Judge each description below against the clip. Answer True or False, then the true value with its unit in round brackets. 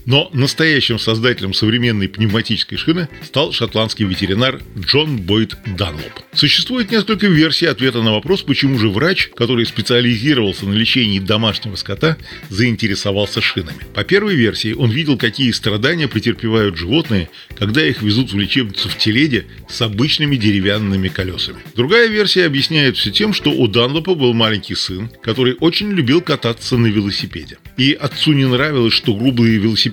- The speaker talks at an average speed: True (145 wpm)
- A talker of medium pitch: False (120 Hz)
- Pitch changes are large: False (5.0 semitones)